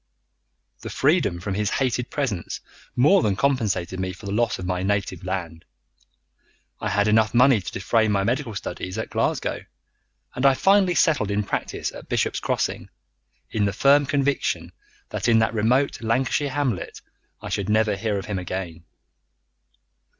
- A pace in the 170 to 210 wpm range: No, average, 160 wpm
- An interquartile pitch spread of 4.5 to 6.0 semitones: Yes, average, 5.1 semitones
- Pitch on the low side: Yes, low, 110 Hz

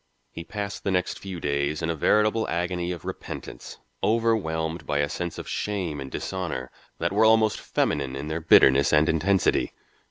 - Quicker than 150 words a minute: Yes, average, 170 wpm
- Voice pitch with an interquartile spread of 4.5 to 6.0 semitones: Yes, average, 4.8 semitones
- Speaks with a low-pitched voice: Yes, very low, 85 Hz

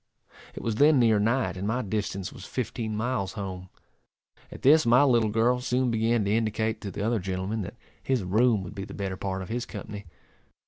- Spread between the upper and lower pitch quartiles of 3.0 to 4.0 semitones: Yes, average, 3.5 semitones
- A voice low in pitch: Yes, low, 110 Hz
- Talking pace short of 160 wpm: No, average, 200 wpm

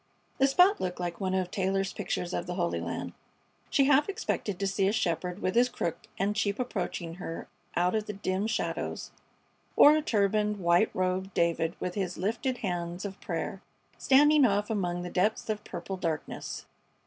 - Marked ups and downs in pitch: No, average, 3.4 semitones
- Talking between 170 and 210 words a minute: Yes, average, 180 wpm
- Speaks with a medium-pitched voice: No, high, 195 Hz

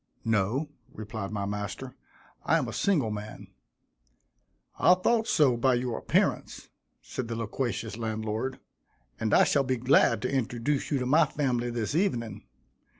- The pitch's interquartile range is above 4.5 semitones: No, average, 3.8 semitones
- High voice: No, low, 120 Hz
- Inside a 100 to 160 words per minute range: Yes, average, 150 wpm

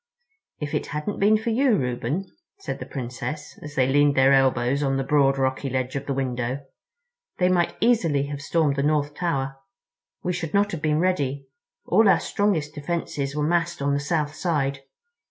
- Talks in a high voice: No, medium, 145 Hz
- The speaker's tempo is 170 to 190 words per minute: Yes, average, 175 wpm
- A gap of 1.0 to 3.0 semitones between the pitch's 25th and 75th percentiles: No, average, 4.0 semitones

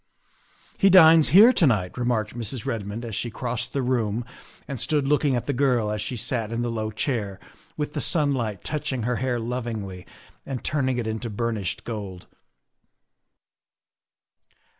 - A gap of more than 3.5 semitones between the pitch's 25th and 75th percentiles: Yes, average, 3.9 semitones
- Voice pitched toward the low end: Yes, low, 120 Hz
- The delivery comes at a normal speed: Yes, average, 160 wpm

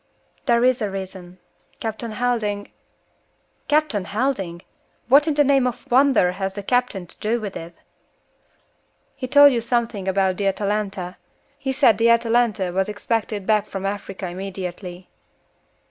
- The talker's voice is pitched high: Yes, high, 210 Hz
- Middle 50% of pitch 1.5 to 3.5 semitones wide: No, average, 4.2 semitones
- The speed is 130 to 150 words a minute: Yes, average, 145 wpm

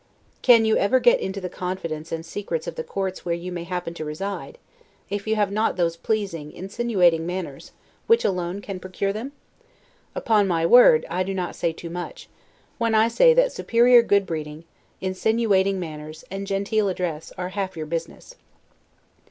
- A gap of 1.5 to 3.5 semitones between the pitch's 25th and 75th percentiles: No, average, 4.3 semitones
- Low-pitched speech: No, high, 190 Hz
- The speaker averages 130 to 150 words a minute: No, average, 175 wpm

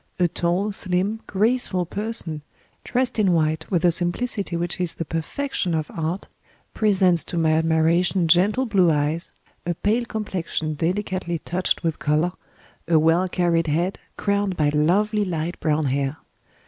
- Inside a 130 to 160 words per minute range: Yes, average, 145 wpm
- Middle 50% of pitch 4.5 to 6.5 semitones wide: No, average, 3.6 semitones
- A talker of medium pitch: Yes, medium, 175 Hz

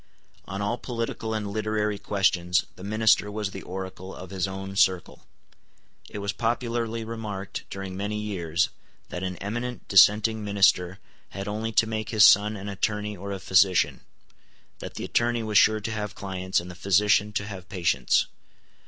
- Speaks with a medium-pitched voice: No, low, 100 Hz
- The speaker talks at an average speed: Yes, average, 165 wpm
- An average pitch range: No, narrow, 2.2 semitones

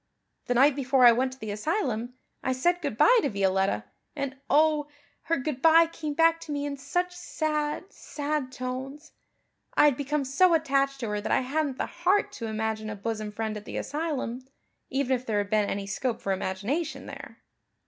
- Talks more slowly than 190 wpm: No, average, 195 wpm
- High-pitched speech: Yes, very high, 270 Hz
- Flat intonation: No, wide, 5.5 semitones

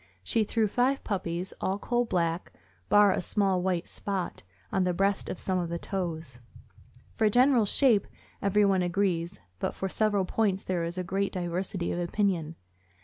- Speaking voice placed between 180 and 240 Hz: Yes, high, 190 Hz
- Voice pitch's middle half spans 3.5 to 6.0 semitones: No, average, 2.9 semitones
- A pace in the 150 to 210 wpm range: Yes, average, 160 wpm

